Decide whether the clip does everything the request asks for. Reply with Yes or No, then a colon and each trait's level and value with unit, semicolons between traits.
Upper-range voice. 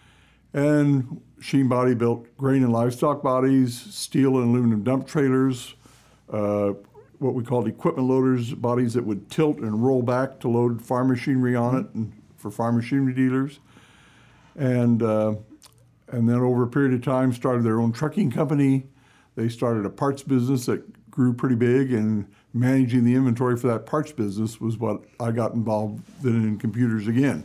No: low, 125 Hz